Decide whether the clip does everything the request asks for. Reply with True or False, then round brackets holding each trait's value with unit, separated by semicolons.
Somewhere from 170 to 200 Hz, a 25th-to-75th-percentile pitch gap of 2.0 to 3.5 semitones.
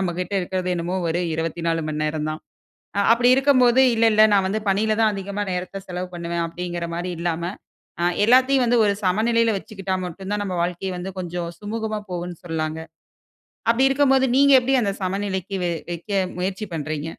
False (190 Hz; 4.0 semitones)